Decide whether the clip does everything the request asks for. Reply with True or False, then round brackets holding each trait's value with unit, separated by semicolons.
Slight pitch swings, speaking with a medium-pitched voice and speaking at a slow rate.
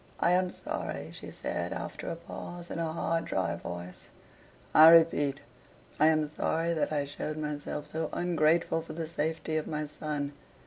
False (1.9 semitones; 155 Hz; 170 wpm)